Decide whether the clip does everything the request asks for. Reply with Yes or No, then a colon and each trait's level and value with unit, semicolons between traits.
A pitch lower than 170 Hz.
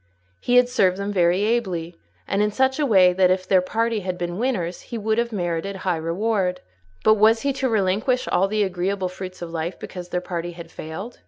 No: high, 190 Hz